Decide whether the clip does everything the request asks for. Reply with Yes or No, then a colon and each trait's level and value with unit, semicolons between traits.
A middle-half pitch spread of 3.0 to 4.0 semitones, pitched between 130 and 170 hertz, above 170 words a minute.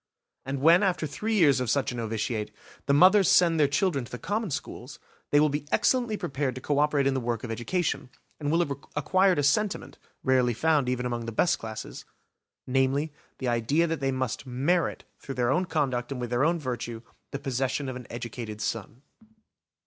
No: average, 4.6 semitones; low, 135 Hz; average, 200 wpm